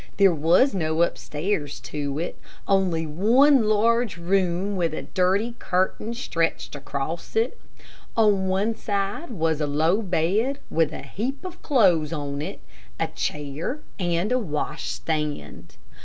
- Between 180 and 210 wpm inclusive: No, average, 140 wpm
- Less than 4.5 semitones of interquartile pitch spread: No, average, 5.3 semitones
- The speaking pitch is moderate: Yes, medium, 180 Hz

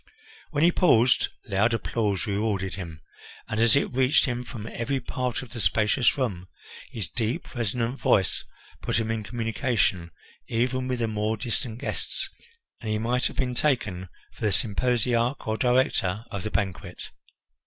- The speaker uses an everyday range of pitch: Yes, average, 3.1 semitones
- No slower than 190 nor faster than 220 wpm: No, average, 160 wpm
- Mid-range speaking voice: No, low, 115 Hz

